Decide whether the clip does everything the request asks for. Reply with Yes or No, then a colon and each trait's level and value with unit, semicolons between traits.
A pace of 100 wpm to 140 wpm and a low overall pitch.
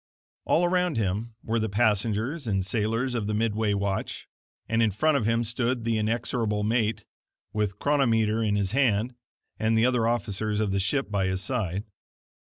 No: average, 175 wpm; low, 110 Hz